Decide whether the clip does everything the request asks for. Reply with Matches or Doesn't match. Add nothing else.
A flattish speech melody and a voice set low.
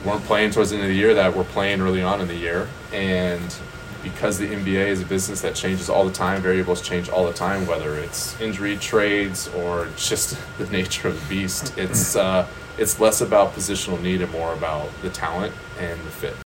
Matches